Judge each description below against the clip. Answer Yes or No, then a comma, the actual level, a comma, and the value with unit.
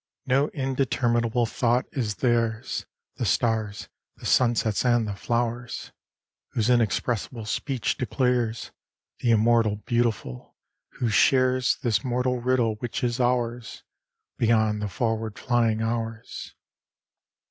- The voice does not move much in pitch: Yes, narrow, 1.9 semitones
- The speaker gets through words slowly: Yes, slow, 110 wpm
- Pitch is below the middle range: Yes, low, 120 Hz